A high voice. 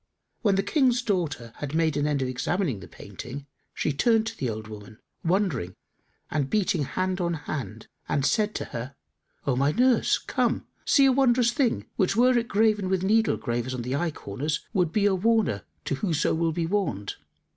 No: medium, 170 Hz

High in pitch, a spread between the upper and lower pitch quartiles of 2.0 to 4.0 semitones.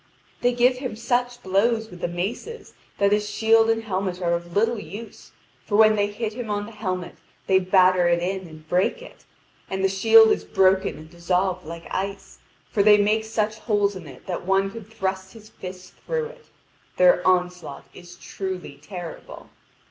Yes: high, 195 Hz; average, 3.4 semitones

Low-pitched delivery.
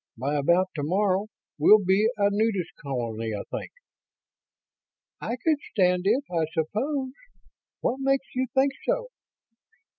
No: high, 200 Hz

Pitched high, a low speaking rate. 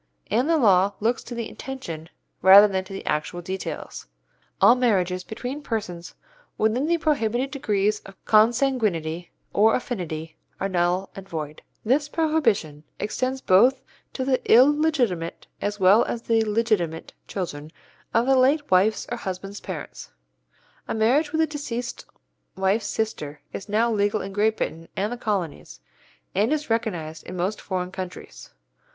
No: high, 215 Hz; average, 150 wpm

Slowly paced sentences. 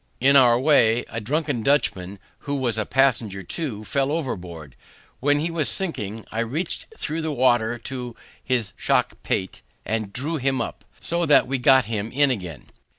No: average, 170 wpm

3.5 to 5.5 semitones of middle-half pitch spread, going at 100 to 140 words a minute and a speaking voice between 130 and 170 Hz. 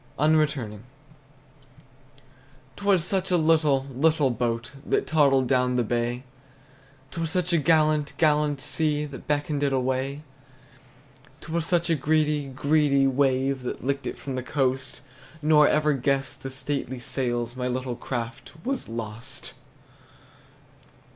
No: average, 3.1 semitones; slow, 135 wpm; medium, 140 Hz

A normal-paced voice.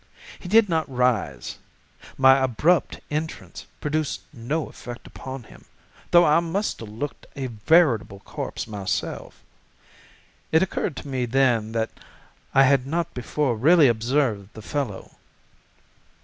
No: slow, 130 wpm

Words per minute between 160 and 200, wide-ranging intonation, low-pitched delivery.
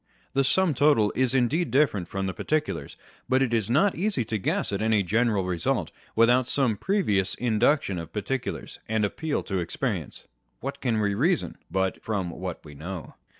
Yes: average, 175 wpm; wide, 5.8 semitones; low, 110 Hz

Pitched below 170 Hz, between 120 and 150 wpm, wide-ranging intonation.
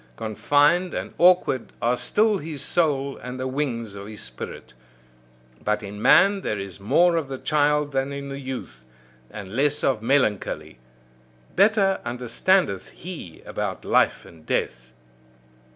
Yes: low, 135 Hz; average, 140 wpm; wide, 6.6 semitones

